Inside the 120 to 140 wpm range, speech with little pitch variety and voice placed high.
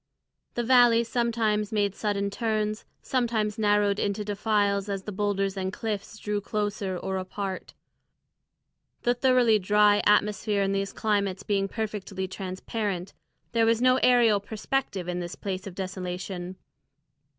Yes: slow, 135 wpm; narrow, 2.1 semitones; high, 205 Hz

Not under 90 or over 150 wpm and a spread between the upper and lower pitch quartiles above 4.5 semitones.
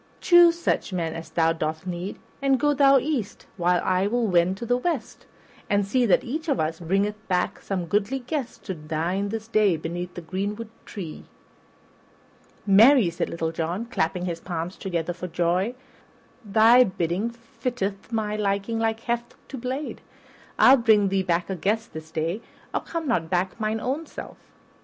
No: average, 170 wpm; average, 5.1 semitones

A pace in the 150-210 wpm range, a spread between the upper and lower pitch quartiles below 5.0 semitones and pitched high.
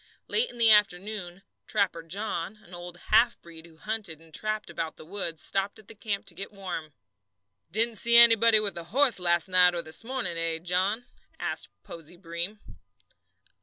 Yes: average, 175 wpm; average, 4.2 semitones; high, 195 Hz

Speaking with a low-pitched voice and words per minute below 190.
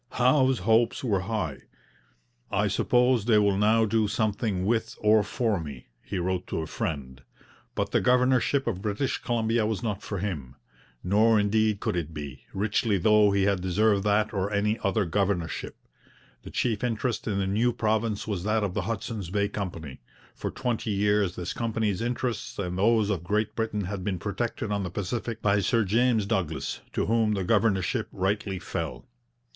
Yes: low, 105 Hz; average, 175 wpm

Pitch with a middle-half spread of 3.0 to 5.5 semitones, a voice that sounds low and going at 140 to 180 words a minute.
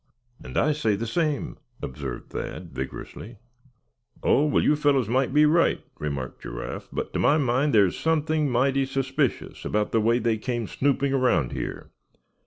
Yes: average, 5.0 semitones; low, 130 Hz; average, 160 wpm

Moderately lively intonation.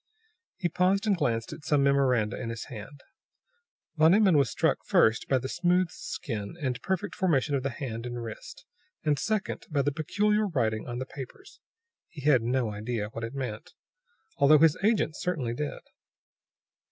No: wide, 6.4 semitones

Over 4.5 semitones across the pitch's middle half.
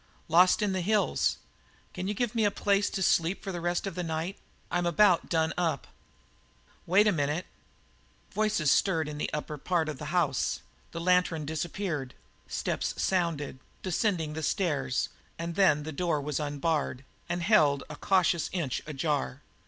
No: average, 3.7 semitones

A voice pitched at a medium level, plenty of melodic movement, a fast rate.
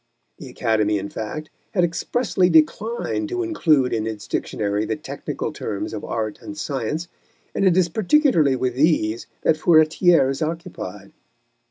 No: medium, 155 Hz; wide, 7.9 semitones; average, 150 wpm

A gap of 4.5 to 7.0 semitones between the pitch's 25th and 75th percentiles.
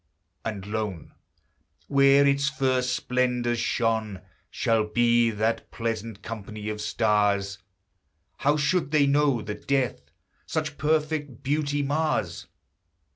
Yes: average, 4.8 semitones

